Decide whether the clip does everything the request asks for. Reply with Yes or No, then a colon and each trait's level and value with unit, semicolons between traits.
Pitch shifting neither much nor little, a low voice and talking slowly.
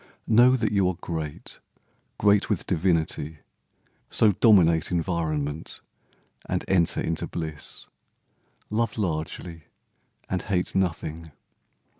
Yes: average, 3.9 semitones; very low, 85 Hz; slow, 100 wpm